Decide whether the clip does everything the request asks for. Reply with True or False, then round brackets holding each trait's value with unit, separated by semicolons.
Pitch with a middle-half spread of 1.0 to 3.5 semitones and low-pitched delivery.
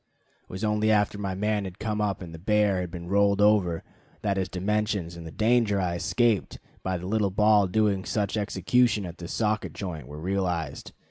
True (2.8 semitones; 100 Hz)